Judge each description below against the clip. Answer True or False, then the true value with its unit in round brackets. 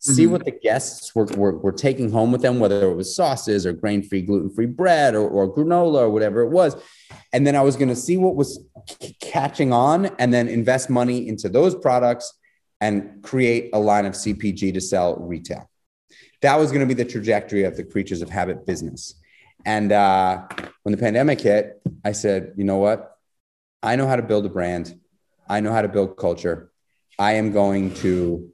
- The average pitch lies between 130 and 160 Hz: False (110 Hz)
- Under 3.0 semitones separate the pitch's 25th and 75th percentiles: False (4.0 semitones)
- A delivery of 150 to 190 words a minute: False (205 wpm)